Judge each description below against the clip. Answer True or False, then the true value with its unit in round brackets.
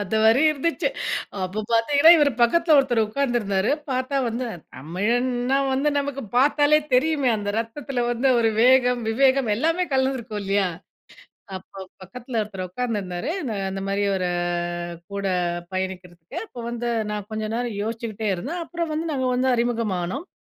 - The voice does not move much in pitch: False (4.9 semitones)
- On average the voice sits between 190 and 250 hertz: True (240 Hz)